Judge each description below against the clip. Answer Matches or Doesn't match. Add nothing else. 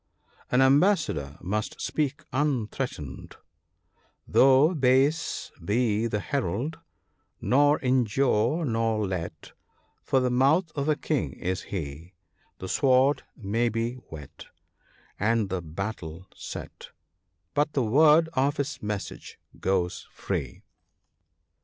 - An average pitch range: Doesn't match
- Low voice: Matches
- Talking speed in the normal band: Doesn't match